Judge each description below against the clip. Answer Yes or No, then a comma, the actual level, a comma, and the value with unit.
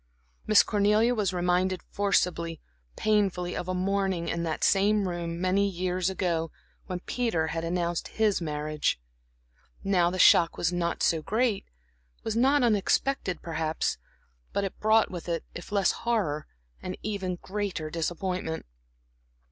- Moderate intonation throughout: Yes, average, 3.1 semitones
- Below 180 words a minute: Yes, average, 140 wpm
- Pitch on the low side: No, medium, 185 Hz